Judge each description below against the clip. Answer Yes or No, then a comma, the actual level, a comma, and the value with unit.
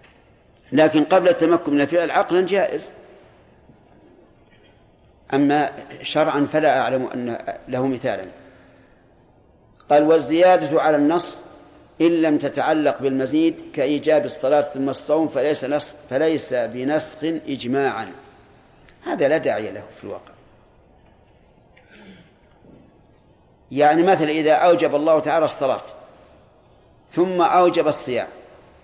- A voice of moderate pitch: Yes, medium, 155 Hz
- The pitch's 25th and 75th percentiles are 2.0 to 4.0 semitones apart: Yes, narrow, 2.4 semitones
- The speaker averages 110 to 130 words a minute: No, average, 100 wpm